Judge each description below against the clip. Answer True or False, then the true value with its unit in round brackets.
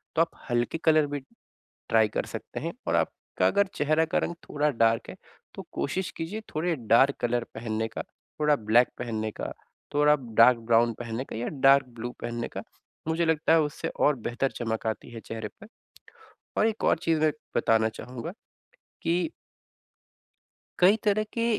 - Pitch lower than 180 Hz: True (135 Hz)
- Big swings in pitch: True (5.7 semitones)